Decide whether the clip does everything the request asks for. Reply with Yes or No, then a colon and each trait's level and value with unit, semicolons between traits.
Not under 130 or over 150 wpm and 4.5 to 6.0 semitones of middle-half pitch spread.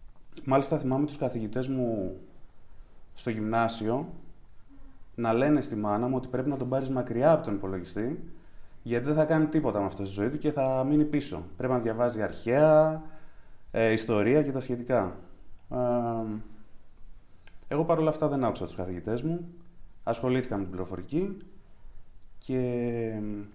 Yes: average, 145 wpm; average, 5.3 semitones